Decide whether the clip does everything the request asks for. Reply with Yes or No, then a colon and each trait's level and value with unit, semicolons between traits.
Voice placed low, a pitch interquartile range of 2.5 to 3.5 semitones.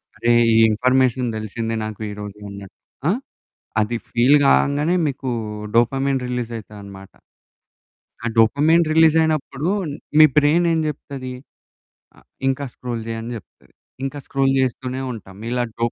No: low, 125 Hz; average, 4.0 semitones